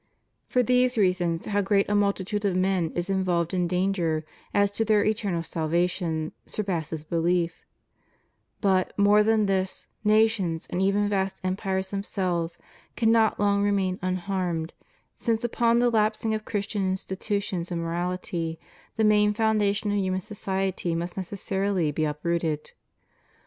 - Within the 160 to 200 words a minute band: No, average, 140 wpm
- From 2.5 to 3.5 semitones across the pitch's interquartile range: Yes, average, 3.0 semitones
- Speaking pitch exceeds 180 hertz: Yes, high, 190 Hz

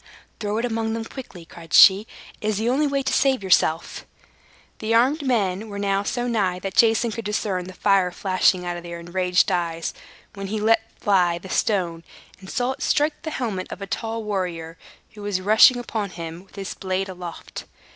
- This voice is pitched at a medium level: No, high, 200 Hz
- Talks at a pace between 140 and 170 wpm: No, average, 195 wpm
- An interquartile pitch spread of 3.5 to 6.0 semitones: Yes, average, 3.9 semitones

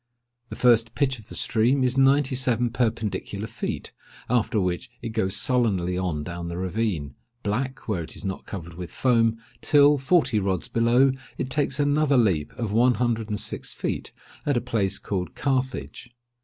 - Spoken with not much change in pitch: No, average, 5.0 semitones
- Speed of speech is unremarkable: Yes, average, 165 wpm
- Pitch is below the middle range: Yes, low, 115 Hz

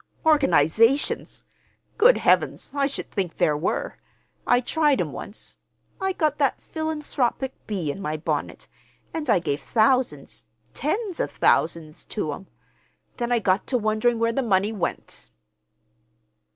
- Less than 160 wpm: Yes, average, 140 wpm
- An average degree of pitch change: No, wide, 7.6 semitones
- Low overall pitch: No, high, 235 Hz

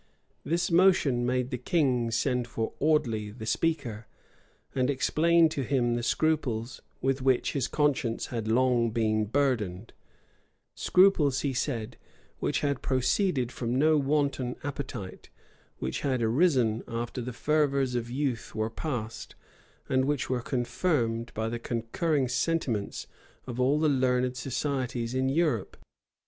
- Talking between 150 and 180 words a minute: No, slow, 135 wpm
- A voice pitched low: Yes, low, 130 Hz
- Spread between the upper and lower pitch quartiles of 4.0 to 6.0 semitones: No, average, 3.5 semitones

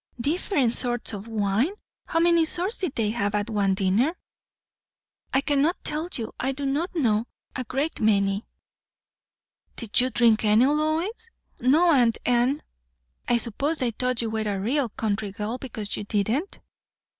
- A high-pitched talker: Yes, high, 245 Hz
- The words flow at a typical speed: Yes, average, 155 wpm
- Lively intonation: Yes, wide, 5.7 semitones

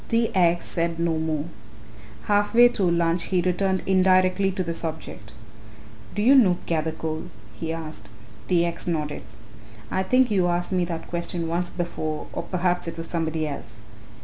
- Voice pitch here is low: No, medium, 170 Hz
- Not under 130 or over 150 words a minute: No, average, 165 wpm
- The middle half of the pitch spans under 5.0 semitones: Yes, narrow, 2.4 semitones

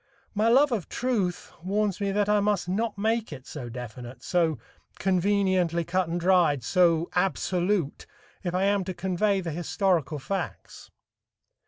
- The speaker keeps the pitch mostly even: No, average, 3.3 semitones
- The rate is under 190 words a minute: Yes, average, 150 wpm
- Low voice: No, medium, 185 Hz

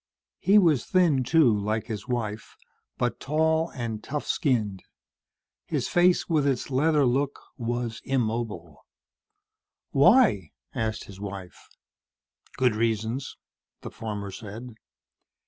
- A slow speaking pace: Yes, slow, 110 wpm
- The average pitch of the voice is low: Yes, low, 120 Hz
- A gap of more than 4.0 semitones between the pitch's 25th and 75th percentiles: Yes, average, 5.0 semitones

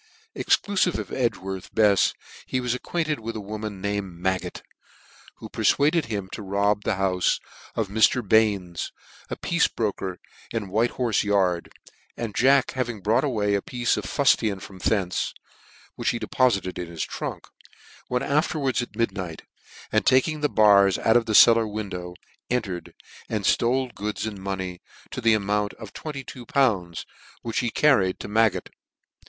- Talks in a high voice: No, low, 110 Hz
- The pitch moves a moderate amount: Yes, average, 4.0 semitones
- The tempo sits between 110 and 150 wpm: No, average, 160 wpm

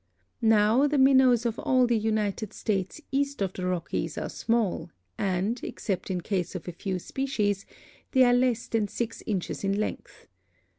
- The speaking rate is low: No, average, 165 wpm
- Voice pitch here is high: Yes, high, 215 Hz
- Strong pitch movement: No, average, 4.3 semitones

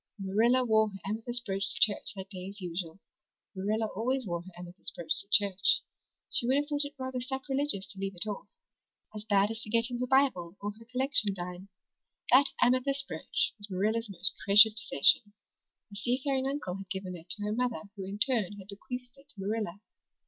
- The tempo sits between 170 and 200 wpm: Yes, average, 190 wpm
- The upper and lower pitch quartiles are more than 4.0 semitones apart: Yes, average, 4.4 semitones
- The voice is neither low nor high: No, high, 210 Hz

